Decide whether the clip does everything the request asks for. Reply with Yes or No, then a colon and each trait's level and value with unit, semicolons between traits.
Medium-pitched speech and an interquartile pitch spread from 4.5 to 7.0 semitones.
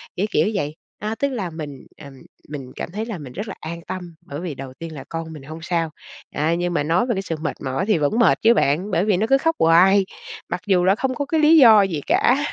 Yes: medium, 175 Hz; average, 5.3 semitones